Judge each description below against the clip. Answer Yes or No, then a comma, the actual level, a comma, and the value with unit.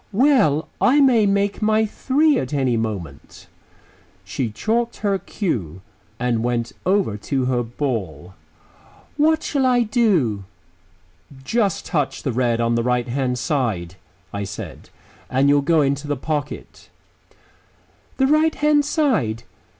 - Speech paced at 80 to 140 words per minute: Yes, slow, 135 wpm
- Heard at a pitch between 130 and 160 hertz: Yes, medium, 140 Hz